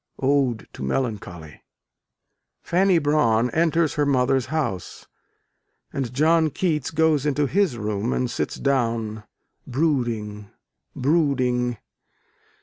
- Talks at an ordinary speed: No, slow, 100 wpm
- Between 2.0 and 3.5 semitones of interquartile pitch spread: No, average, 4.9 semitones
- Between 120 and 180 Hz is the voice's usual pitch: Yes, low, 135 Hz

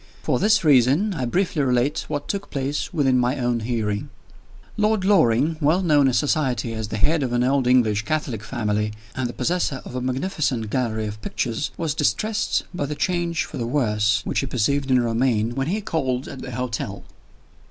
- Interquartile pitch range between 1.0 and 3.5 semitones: No, average, 4.7 semitones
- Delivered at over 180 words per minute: Yes, average, 190 wpm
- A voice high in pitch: No, low, 130 Hz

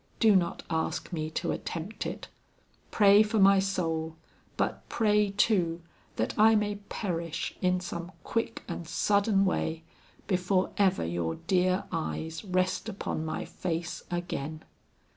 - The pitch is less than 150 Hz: No, medium, 185 Hz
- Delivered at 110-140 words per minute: Yes, slow, 135 wpm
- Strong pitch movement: No, average, 3.5 semitones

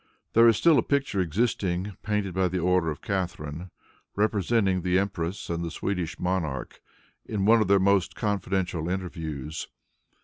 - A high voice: No, very low, 95 Hz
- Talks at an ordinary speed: Yes, average, 145 wpm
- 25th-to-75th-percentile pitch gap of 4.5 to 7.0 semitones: No, average, 3.0 semitones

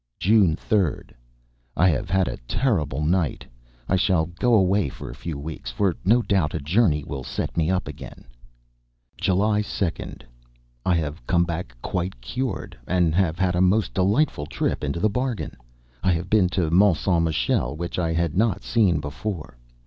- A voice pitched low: Yes, very low, 90 Hz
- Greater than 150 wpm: Yes, average, 170 wpm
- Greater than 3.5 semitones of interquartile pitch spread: Yes, average, 4.0 semitones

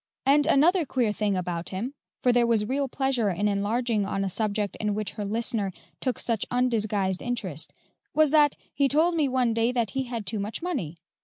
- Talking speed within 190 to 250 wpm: Yes, average, 200 wpm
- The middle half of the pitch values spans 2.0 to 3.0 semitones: No, average, 4.7 semitones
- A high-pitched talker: Yes, high, 230 Hz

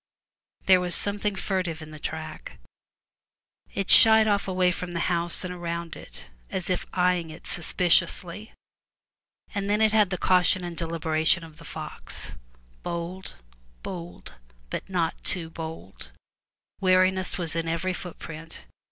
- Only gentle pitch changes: Yes, narrow, 2.3 semitones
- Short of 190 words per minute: Yes, average, 145 wpm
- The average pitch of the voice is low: No, medium, 175 Hz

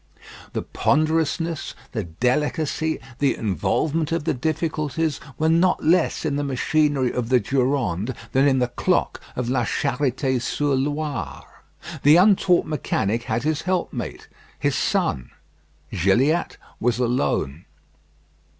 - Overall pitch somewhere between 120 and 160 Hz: Yes, medium, 140 Hz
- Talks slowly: Yes, slow, 125 wpm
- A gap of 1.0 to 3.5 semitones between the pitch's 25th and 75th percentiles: No, average, 4.3 semitones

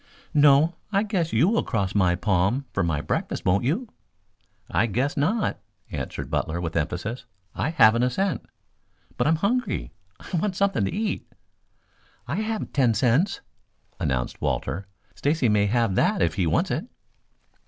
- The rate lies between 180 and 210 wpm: No, average, 155 wpm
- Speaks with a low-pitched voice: Yes, low, 125 Hz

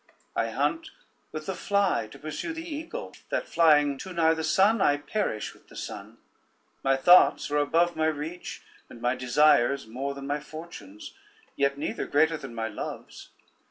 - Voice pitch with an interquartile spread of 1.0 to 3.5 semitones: No, average, 4.5 semitones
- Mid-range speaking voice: Yes, medium, 155 Hz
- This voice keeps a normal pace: Yes, average, 170 wpm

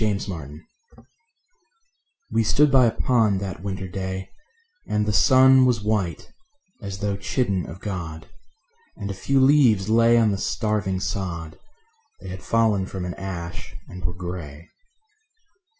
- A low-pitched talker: Yes, low, 100 Hz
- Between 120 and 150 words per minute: Yes, average, 145 wpm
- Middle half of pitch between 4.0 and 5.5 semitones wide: No, average, 3.4 semitones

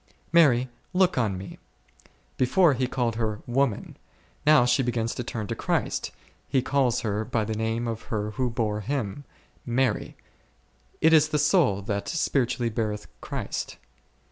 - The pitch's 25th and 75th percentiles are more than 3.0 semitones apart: Yes, average, 3.8 semitones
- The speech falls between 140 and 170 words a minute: Yes, average, 150 wpm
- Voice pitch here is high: No, low, 120 Hz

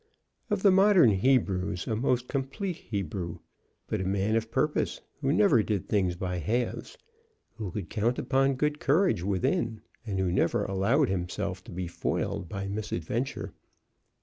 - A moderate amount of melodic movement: No, wide, 6.1 semitones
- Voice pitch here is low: Yes, low, 110 Hz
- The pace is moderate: Yes, average, 150 wpm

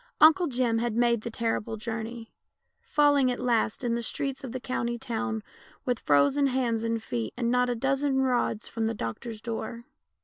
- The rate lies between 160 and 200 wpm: Yes, average, 175 wpm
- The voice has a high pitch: Yes, high, 235 Hz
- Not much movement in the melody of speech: Yes, narrow, 2.3 semitones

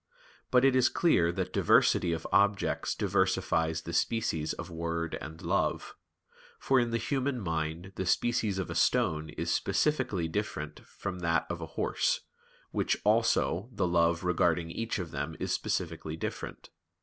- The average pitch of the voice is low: Yes, very low, 85 Hz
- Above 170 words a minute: No, average, 155 wpm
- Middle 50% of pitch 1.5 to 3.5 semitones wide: No, wide, 5.4 semitones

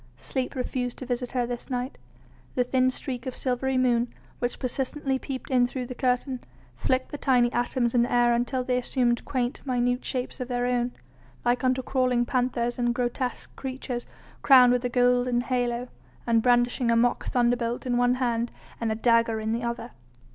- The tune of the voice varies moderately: No, narrow, 1.1 semitones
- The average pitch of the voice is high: Yes, high, 245 Hz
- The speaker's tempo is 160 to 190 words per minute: Yes, average, 185 wpm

